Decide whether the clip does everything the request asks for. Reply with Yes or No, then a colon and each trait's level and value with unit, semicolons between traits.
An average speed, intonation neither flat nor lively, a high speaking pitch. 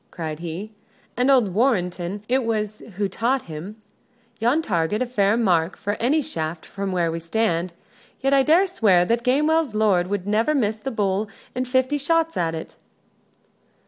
No: average, 175 wpm; wide, 6.2 semitones; high, 215 Hz